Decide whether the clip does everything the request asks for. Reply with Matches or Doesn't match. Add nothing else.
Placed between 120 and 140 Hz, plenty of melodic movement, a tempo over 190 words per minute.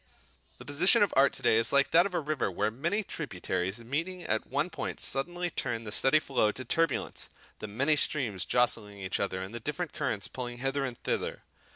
Matches